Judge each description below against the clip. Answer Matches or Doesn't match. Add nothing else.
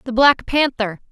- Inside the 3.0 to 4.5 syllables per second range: Matches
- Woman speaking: Matches